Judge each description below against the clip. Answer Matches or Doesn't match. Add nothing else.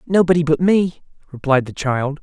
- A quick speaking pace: Doesn't match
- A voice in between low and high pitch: Matches